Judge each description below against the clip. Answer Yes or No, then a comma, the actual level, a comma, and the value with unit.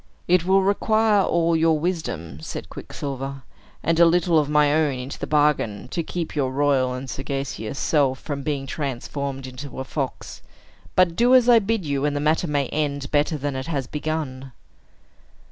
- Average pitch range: Yes, average, 3.5 semitones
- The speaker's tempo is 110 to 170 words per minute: No, average, 180 wpm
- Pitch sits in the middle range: Yes, medium, 145 Hz